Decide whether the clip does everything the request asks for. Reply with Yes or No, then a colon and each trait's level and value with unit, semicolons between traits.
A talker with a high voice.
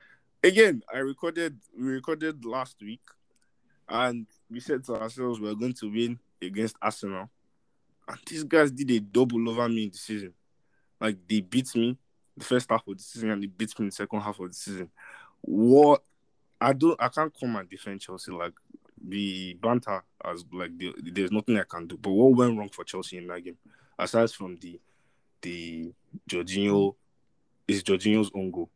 No: low, 110 Hz